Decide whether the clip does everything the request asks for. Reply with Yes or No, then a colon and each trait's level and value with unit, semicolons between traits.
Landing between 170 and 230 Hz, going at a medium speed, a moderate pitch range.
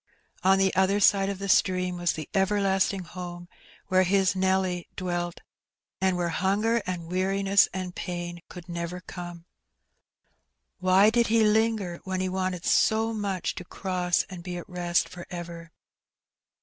No: medium, 185 Hz; average, 155 wpm; narrow, 1.8 semitones